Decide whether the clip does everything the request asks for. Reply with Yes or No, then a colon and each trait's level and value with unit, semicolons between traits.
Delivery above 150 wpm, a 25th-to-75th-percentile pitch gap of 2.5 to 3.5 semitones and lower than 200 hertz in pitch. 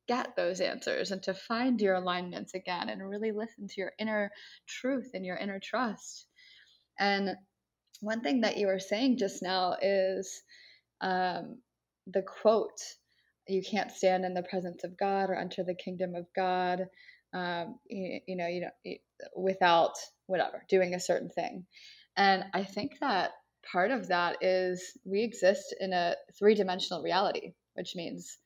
Yes: average, 160 wpm; average, 2.9 semitones; high, 190 Hz